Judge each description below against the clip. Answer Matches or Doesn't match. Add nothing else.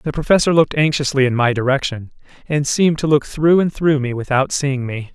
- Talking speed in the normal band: Doesn't match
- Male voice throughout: Matches